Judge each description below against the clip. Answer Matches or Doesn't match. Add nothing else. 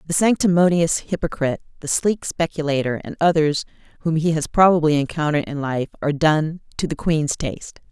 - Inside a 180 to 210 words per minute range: Doesn't match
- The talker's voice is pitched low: Doesn't match